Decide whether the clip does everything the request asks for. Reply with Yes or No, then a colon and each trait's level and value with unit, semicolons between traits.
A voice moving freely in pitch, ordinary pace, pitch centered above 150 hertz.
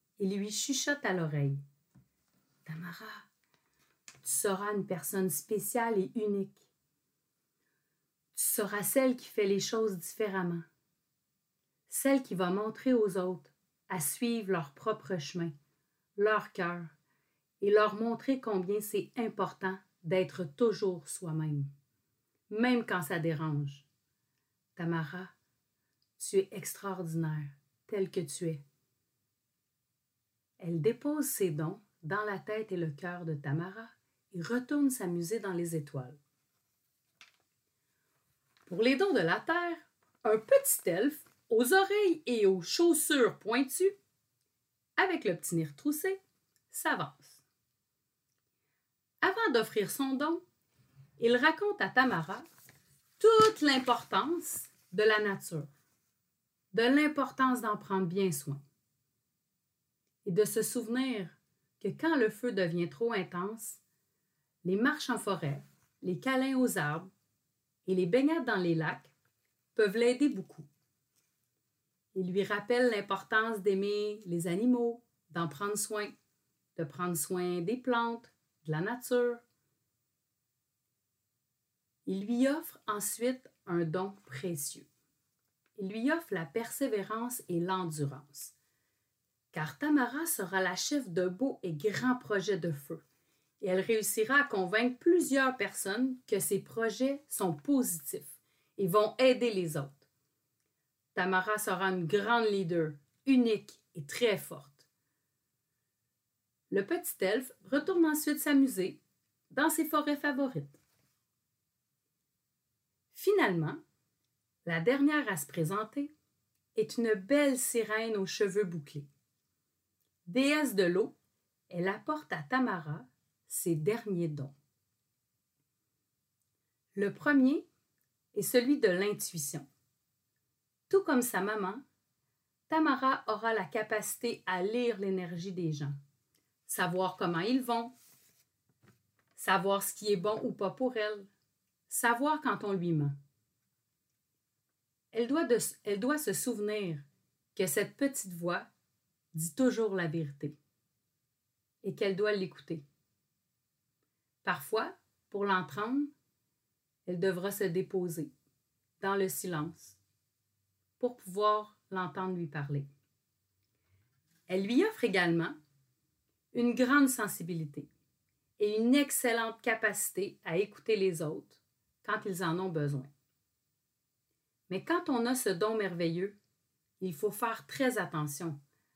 No: wide, 7.5 semitones; slow, 115 wpm; high, 190 Hz